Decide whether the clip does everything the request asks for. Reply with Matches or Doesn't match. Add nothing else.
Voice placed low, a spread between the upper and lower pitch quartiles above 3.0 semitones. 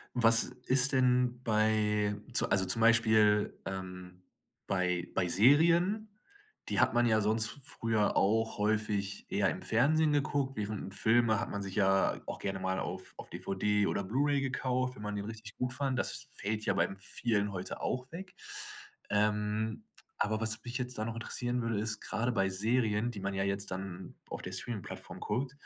Matches